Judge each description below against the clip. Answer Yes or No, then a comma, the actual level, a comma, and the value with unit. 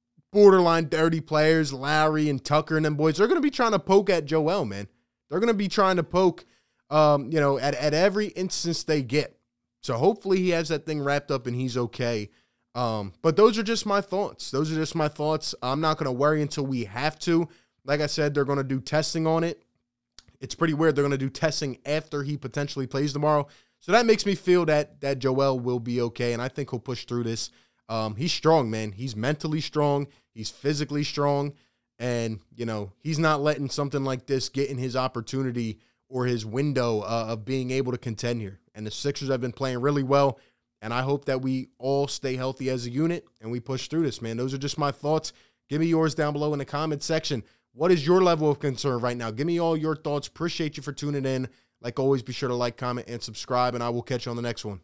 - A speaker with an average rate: No, fast, 235 wpm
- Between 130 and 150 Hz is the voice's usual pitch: Yes, medium, 140 Hz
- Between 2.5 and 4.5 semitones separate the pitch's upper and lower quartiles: Yes, average, 4.0 semitones